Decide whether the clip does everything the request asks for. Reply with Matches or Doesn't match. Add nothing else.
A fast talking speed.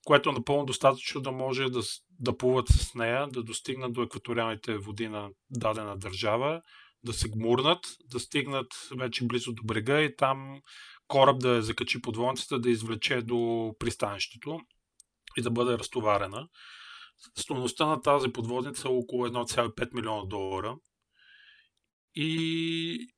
Doesn't match